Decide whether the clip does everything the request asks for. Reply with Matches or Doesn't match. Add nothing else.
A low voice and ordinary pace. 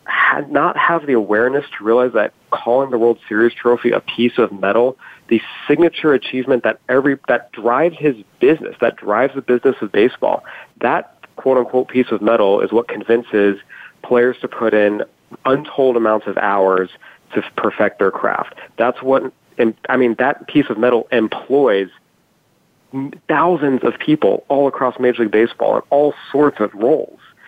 Matches